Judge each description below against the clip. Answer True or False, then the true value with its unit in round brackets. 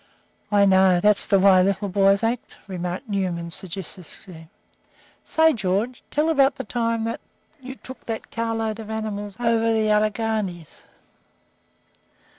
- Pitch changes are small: False (3.2 semitones)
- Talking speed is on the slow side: True (130 wpm)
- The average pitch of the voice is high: True (210 Hz)